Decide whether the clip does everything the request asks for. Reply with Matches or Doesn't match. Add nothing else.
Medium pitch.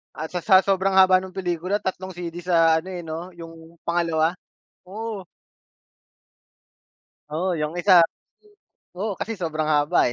Matches